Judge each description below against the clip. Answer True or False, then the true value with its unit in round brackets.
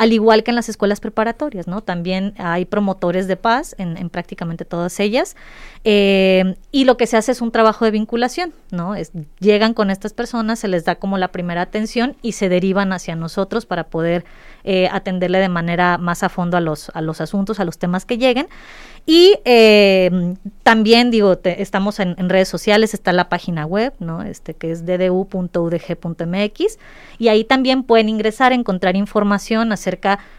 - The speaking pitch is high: True (195 Hz)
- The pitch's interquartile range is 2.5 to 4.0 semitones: True (3.7 semitones)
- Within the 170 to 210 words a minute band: True (185 wpm)